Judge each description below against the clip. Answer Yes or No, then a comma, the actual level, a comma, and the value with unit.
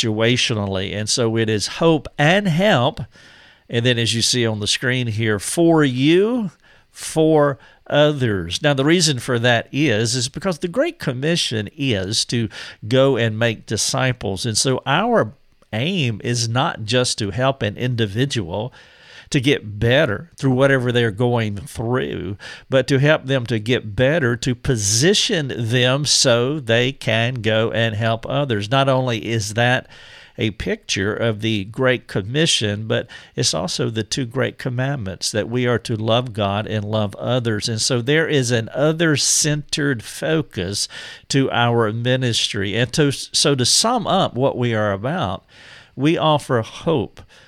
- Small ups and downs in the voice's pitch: No, average, 4.0 semitones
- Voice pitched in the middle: No, low, 125 Hz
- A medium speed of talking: Yes, average, 155 wpm